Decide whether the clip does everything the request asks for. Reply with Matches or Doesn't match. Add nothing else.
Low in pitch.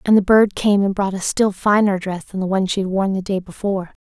Doesn't match